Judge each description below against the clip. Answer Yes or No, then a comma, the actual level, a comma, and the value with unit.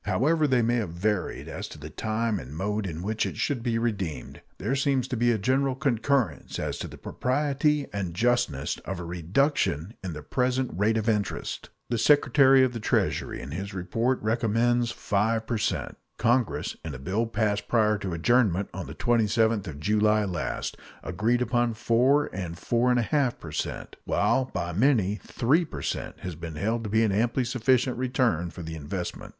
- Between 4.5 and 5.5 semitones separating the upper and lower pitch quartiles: Yes, average, 4.8 semitones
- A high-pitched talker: No, low, 110 Hz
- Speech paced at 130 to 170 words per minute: No, average, 185 wpm